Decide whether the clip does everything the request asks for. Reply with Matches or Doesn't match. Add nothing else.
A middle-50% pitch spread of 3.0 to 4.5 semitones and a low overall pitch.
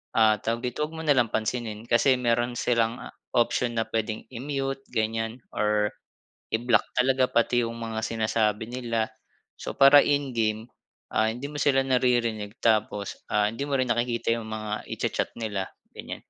Doesn't match